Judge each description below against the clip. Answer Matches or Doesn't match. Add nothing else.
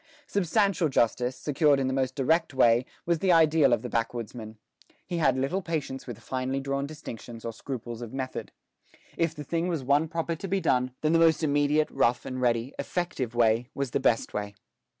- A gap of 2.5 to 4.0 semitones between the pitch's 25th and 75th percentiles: Doesn't match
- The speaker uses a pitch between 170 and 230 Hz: Doesn't match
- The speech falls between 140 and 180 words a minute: Doesn't match